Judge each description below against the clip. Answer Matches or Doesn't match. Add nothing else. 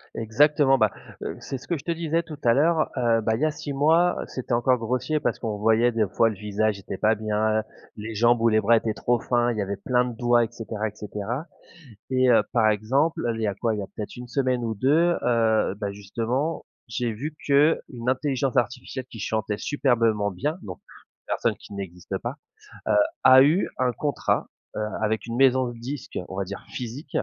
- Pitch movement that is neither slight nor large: Matches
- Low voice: Matches